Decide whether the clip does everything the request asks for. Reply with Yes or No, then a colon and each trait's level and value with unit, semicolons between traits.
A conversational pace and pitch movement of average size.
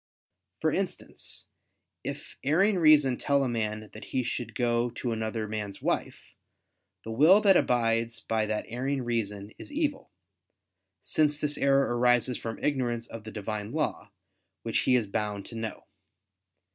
Yes: average, 150 wpm; average, 4.0 semitones